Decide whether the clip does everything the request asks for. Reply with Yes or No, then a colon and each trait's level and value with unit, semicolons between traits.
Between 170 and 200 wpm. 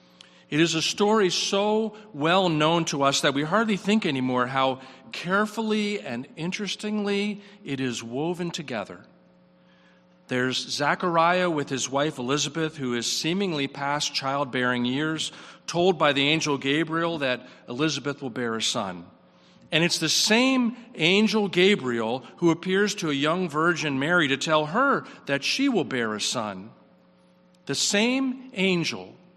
No: average, 145 wpm